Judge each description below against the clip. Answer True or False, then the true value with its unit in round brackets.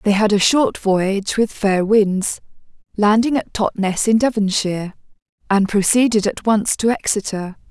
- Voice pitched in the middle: False (210 Hz)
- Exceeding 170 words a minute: False (150 wpm)